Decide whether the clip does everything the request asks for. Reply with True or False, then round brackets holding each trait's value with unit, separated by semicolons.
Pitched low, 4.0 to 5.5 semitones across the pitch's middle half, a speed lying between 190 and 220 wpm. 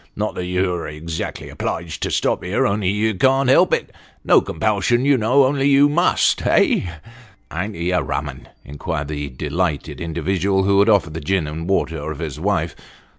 True (95 Hz; 5.1 semitones; 200 wpm)